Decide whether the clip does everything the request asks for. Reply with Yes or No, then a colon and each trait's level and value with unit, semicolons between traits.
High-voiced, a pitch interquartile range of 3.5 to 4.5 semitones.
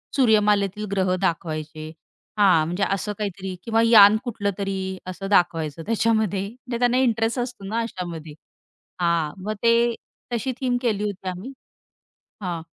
Yes: high, 200 Hz; average, 4.0 semitones